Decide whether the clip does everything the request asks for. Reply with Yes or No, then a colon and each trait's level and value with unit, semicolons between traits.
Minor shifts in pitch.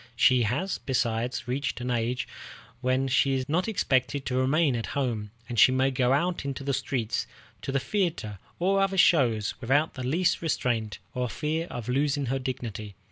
No: average, 3.0 semitones